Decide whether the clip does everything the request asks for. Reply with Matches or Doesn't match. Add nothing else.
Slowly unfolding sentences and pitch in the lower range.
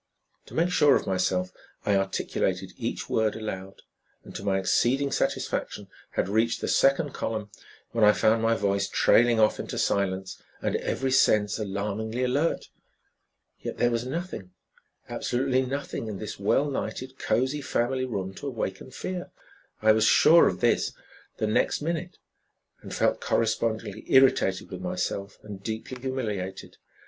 Doesn't match